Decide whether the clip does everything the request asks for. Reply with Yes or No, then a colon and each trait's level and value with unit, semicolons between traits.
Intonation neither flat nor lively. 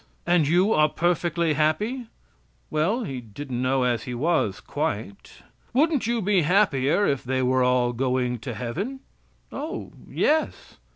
No: wide, 7.9 semitones